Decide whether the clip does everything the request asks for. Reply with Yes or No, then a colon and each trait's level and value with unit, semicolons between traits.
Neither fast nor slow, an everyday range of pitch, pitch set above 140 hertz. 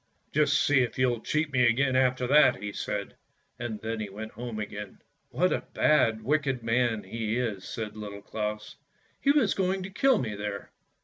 No: average, 195 wpm; average, 4.6 semitones; low, 120 Hz